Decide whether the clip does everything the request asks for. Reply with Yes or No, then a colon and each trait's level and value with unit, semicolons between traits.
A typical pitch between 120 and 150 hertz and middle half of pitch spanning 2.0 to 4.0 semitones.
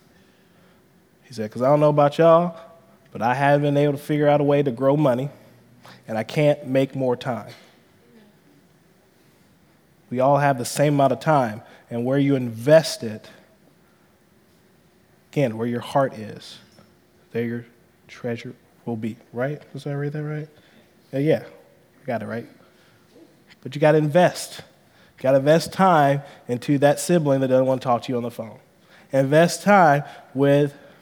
Yes: medium, 140 Hz; average, 3.7 semitones